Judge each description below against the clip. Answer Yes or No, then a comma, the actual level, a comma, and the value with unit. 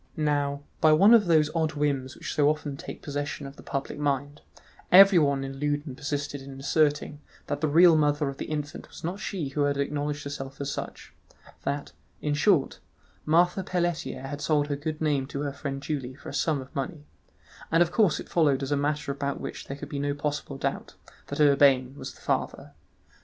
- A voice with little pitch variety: Yes, narrow, 1.6 semitones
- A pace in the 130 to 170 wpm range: No, average, 200 wpm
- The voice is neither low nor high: Yes, medium, 145 Hz